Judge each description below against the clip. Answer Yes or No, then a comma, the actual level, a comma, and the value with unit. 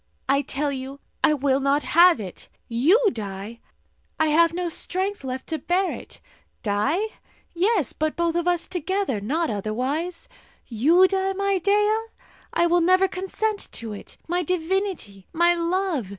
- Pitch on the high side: Yes, very high, 335 Hz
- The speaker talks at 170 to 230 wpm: No, average, 150 wpm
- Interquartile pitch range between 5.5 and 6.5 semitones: Yes, wide, 5.8 semitones